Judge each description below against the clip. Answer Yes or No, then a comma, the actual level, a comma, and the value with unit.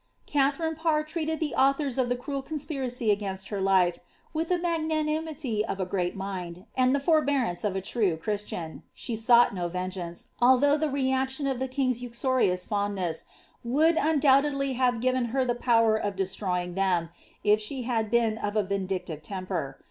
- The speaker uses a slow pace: No, average, 170 wpm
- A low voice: No, high, 240 Hz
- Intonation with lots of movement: Yes, wide, 6.1 semitones